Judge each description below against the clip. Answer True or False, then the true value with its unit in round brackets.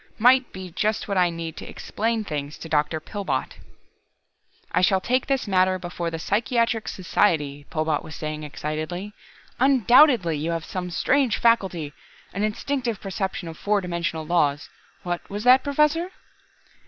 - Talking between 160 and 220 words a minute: False (150 wpm)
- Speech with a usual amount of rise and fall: False (6.0 semitones)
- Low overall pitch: False (185 Hz)